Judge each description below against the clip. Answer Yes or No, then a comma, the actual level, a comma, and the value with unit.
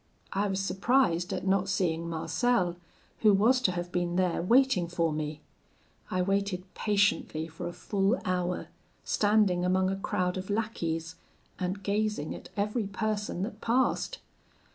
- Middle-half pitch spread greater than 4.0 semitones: No, average, 2.9 semitones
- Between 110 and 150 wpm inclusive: Yes, average, 145 wpm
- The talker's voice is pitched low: No, high, 190 Hz